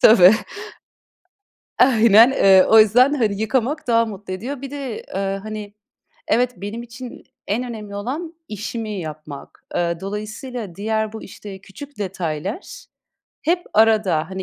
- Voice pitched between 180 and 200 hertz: No, high, 215 Hz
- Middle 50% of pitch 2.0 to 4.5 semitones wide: Yes, average, 3.8 semitones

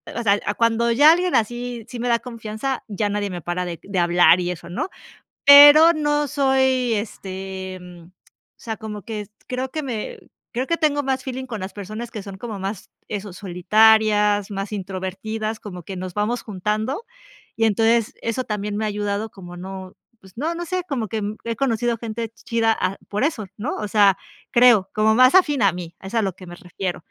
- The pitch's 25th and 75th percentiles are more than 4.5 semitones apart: No, average, 4.1 semitones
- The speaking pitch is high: Yes, high, 215 Hz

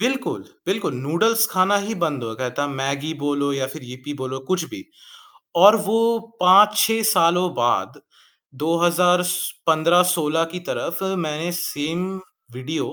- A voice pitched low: No, medium, 170 Hz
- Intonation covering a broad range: No, average, 4.4 semitones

